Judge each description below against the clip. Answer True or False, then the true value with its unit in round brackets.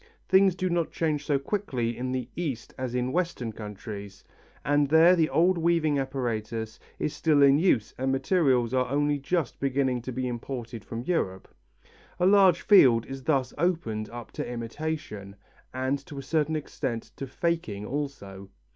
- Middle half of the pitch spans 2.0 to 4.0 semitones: False (5.1 semitones)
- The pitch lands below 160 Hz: True (135 Hz)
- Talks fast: False (165 wpm)